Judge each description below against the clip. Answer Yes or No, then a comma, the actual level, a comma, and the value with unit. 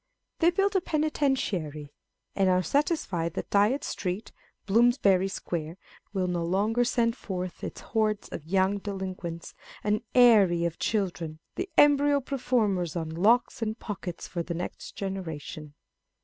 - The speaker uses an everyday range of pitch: No, wide, 5.7 semitones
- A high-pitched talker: Yes, high, 195 Hz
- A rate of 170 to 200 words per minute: No, average, 140 wpm